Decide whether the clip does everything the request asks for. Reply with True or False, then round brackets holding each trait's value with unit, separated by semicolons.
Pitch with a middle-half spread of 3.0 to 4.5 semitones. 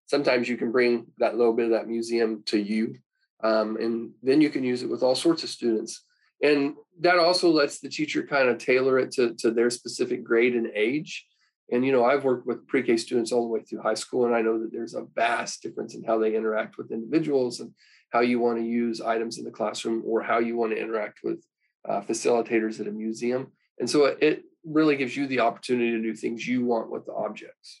False (2.6 semitones)